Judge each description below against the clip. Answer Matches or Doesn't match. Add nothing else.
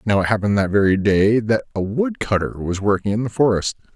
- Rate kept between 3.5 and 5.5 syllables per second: Doesn't match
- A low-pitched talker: Matches